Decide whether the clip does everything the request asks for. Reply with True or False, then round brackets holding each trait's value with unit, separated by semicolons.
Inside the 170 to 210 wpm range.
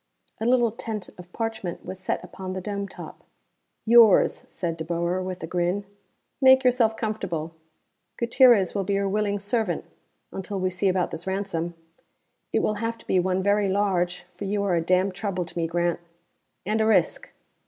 True (180 wpm)